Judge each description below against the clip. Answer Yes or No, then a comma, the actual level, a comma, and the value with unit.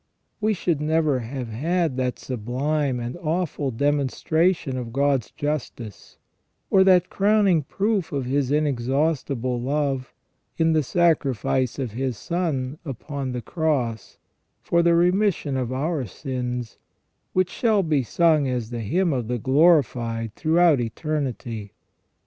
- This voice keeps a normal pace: No, slow, 130 wpm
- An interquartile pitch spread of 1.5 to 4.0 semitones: No, average, 4.7 semitones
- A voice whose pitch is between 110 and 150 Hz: Yes, medium, 140 Hz